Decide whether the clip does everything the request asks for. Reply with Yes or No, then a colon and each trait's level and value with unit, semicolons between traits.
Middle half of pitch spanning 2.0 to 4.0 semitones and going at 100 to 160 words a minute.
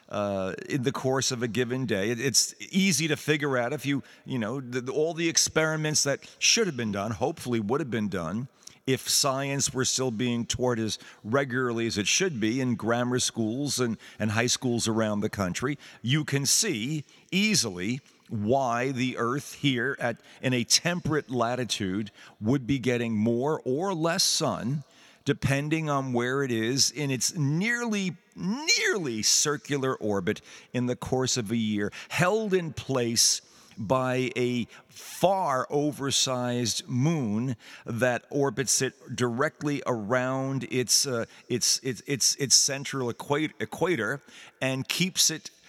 Yes: average, 3.6 semitones; average, 150 wpm